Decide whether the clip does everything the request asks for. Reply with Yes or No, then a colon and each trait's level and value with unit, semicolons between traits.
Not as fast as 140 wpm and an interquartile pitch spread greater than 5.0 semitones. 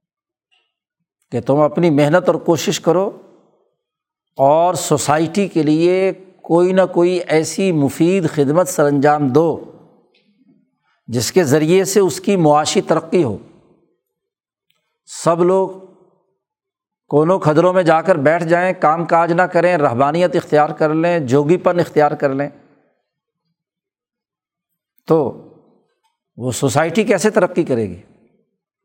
No: average, 120 wpm; average, 3.7 semitones